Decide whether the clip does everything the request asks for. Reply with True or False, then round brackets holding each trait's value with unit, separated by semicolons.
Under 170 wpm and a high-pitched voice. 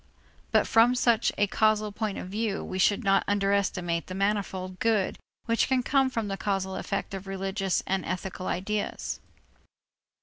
True (160 wpm; 200 Hz)